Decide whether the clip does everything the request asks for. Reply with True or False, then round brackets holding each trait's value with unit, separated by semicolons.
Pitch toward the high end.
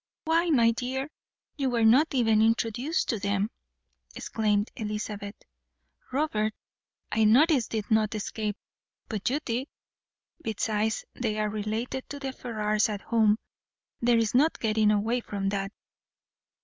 True (220 Hz)